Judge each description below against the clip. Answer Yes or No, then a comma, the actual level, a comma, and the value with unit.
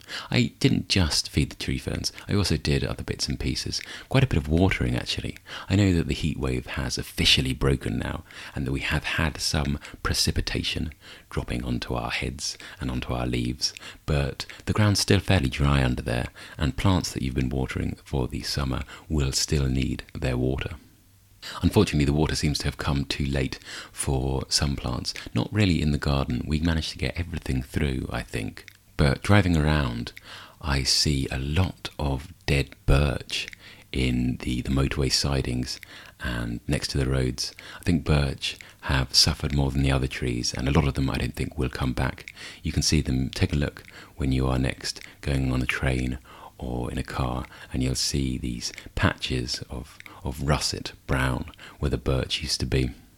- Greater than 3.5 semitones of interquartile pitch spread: Yes, average, 4.5 semitones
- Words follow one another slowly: No, average, 190 wpm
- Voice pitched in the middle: No, very low, 70 Hz